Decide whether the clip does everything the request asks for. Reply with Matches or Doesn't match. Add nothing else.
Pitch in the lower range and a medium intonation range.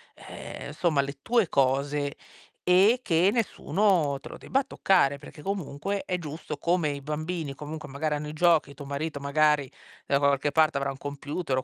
Doesn't match